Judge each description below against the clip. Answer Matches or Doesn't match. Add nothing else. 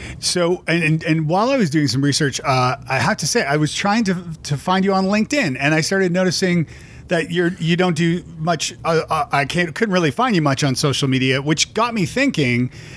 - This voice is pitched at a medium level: Matches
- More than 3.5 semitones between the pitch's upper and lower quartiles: Matches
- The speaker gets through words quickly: Matches